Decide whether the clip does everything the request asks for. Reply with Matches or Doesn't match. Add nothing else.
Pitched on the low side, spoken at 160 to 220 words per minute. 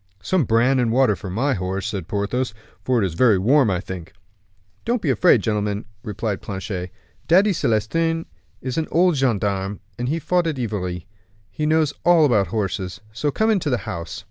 Matches